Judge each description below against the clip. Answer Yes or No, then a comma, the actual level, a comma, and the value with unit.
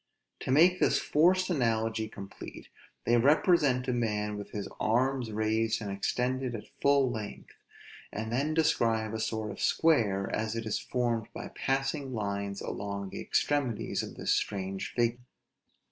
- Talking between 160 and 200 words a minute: No, average, 150 wpm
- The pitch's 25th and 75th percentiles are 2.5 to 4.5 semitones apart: Yes, average, 4.0 semitones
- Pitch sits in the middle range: No, low, 115 Hz